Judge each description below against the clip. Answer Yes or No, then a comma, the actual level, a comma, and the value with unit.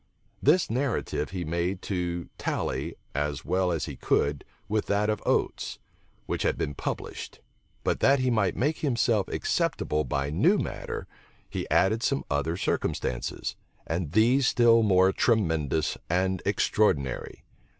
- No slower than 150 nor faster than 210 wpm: No, average, 140 wpm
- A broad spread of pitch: Yes, wide, 5.9 semitones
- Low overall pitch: Yes, very low, 95 Hz